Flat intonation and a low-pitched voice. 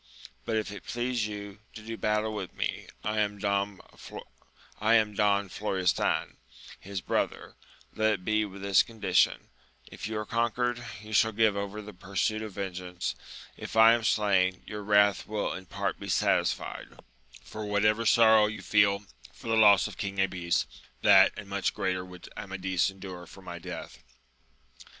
Yes: narrow, 2.0 semitones; low, 105 Hz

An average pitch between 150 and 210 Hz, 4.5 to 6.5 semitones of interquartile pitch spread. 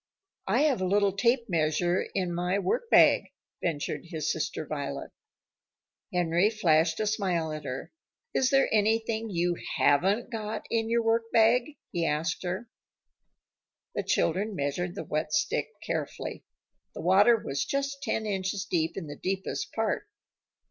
Yes: high, 190 Hz; average, 5.1 semitones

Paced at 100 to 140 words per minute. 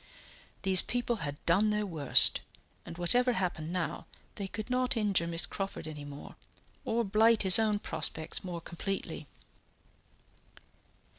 Yes: slow, 135 wpm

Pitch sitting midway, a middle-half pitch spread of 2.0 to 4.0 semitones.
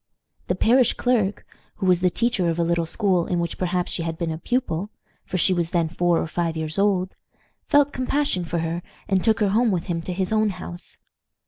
Yes: medium, 180 Hz; average, 3.5 semitones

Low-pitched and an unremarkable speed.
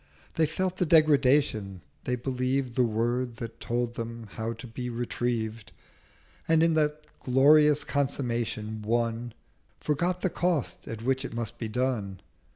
Yes: low, 125 Hz; average, 145 wpm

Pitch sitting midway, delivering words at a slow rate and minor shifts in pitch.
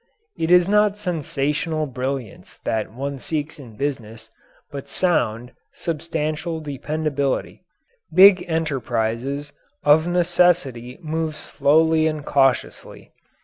No: medium, 150 Hz; slow, 100 wpm; average, 3.4 semitones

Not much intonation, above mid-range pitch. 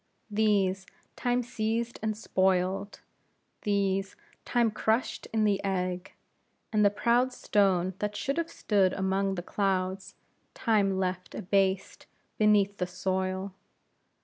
Yes: narrow, 2.3 semitones; high, 195 Hz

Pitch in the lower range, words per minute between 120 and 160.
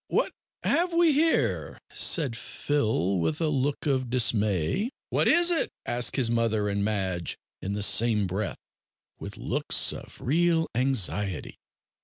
Yes: low, 120 Hz; average, 140 wpm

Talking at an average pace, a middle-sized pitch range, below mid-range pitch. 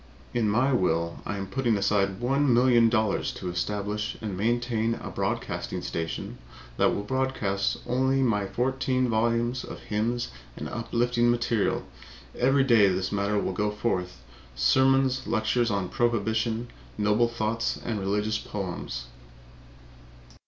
No: slow, 130 wpm; average, 3.1 semitones; low, 110 Hz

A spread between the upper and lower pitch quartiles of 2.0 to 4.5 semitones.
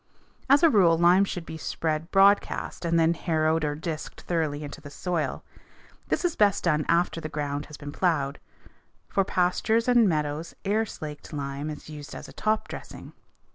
Yes: average, 3.9 semitones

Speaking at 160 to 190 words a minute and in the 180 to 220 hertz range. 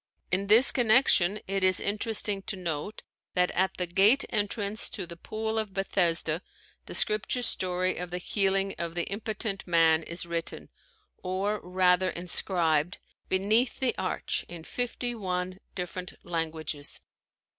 No: average, 140 wpm; medium, 185 Hz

